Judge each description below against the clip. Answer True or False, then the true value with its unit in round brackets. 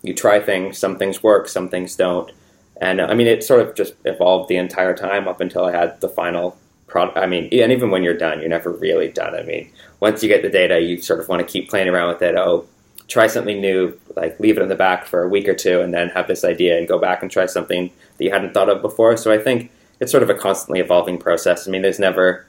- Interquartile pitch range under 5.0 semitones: False (5.6 semitones)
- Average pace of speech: False (270 wpm)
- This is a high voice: False (95 Hz)